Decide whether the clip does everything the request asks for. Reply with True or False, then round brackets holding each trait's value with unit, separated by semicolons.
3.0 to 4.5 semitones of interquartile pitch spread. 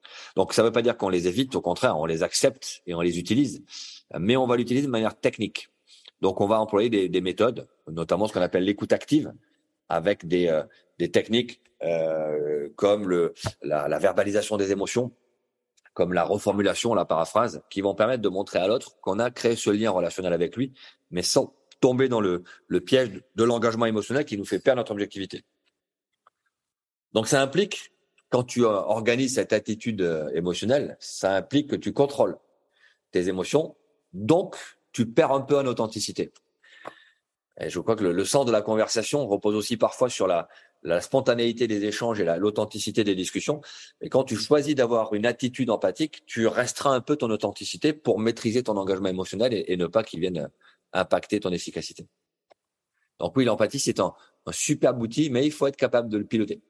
True (4.1 semitones)